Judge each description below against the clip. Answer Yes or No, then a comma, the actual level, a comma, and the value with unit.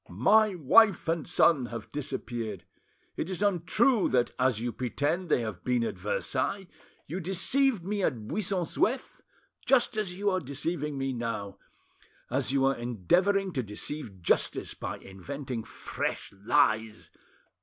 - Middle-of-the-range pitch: Yes, medium, 145 Hz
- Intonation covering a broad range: Yes, wide, 8.2 semitones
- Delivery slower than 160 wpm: Yes, average, 145 wpm